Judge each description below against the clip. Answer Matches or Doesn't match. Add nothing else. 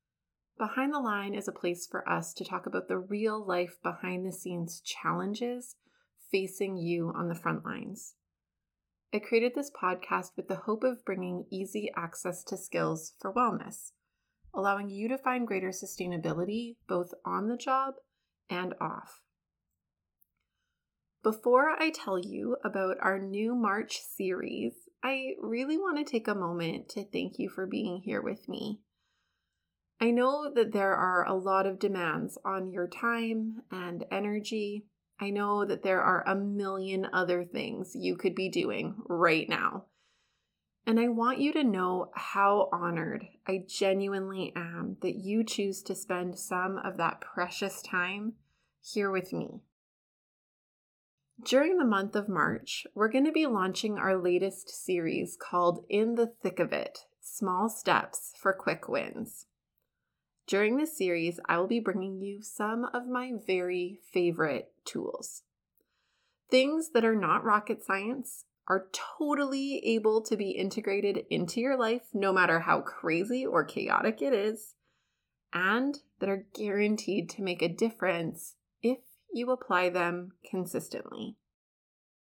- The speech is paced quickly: Doesn't match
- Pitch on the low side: Doesn't match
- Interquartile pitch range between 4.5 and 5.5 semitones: Doesn't match